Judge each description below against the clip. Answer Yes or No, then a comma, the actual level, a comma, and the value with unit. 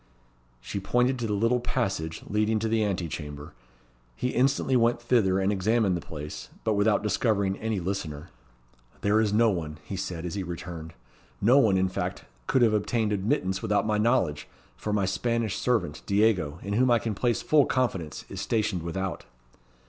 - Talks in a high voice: No, low, 105 Hz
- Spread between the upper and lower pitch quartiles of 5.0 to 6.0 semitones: No, average, 3.7 semitones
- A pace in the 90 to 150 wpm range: No, average, 180 wpm